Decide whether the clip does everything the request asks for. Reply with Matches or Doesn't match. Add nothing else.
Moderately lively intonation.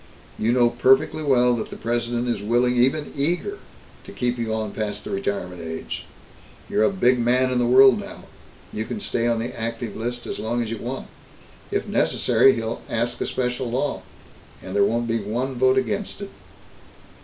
Doesn't match